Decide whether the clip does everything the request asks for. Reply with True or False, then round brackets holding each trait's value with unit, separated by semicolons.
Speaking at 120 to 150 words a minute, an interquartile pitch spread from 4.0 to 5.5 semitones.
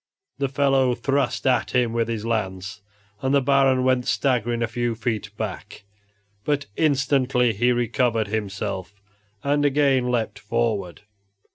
False (135 wpm; 3.4 semitones)